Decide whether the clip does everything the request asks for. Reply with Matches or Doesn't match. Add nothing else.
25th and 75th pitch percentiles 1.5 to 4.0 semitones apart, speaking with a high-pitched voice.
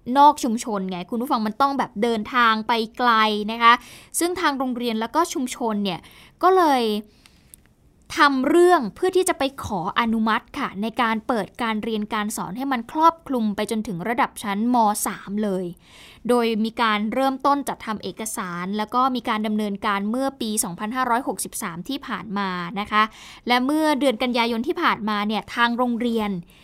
Matches